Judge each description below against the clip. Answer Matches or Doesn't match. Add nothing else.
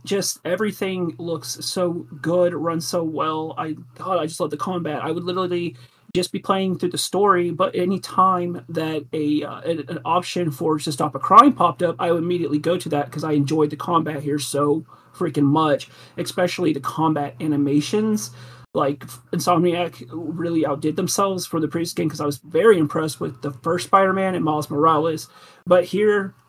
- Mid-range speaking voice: Matches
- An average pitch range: Matches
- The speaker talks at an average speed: Matches